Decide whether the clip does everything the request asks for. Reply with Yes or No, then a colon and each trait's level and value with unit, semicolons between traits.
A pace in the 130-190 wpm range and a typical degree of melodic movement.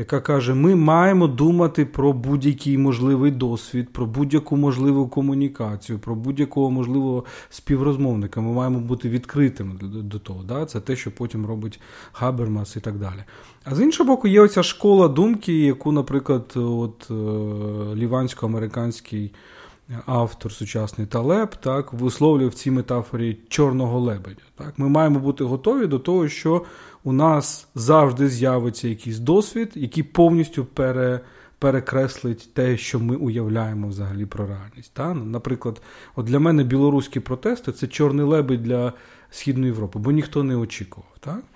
Yes: average, 140 wpm; average, 3.7 semitones